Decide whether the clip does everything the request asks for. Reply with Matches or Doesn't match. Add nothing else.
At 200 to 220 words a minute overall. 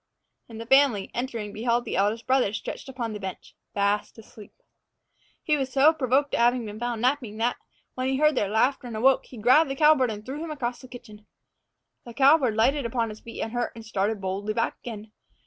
Matches